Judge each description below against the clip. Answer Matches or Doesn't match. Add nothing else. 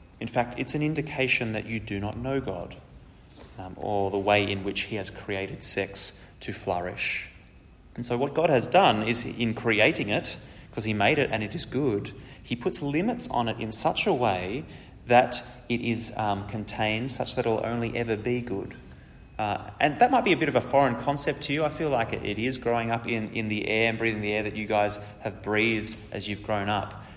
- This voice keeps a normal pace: Doesn't match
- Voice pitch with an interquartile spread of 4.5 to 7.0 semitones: Doesn't match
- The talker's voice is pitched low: Matches